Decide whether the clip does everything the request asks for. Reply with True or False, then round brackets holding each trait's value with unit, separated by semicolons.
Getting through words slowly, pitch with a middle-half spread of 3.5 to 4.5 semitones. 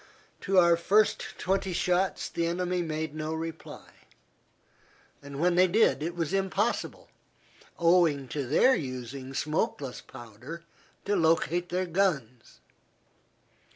True (115 wpm; 4.2 semitones)